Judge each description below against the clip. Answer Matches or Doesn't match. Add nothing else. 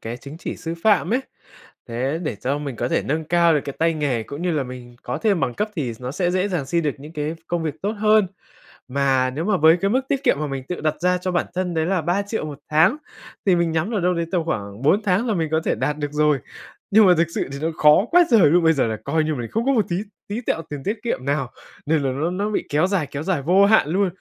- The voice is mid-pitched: Matches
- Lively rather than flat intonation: Doesn't match